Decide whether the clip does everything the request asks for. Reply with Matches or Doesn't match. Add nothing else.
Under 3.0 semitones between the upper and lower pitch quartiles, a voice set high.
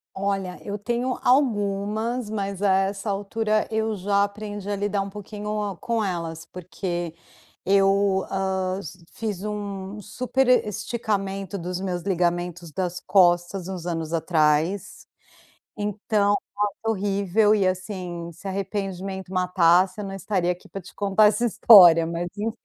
Matches